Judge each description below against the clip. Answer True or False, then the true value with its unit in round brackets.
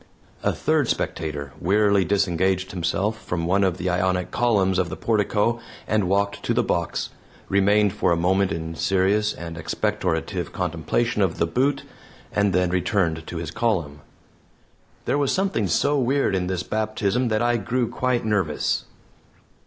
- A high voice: False (95 Hz)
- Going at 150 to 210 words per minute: True (155 wpm)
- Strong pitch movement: False (3.6 semitones)